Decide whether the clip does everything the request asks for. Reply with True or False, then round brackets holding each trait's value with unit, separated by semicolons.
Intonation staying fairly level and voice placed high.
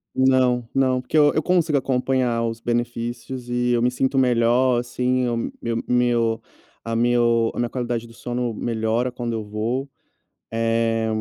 False (1.6 semitones; 120 Hz)